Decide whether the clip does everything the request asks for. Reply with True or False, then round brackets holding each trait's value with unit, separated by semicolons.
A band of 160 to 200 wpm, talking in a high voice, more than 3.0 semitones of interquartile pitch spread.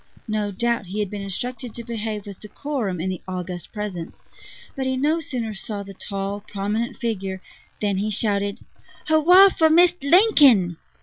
True (165 wpm; 215 Hz; 4.8 semitones)